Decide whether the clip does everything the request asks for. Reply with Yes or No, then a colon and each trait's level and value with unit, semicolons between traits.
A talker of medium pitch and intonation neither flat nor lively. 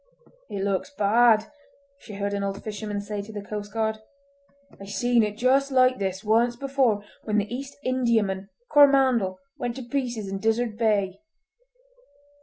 No: high, 220 Hz; average, 3.3 semitones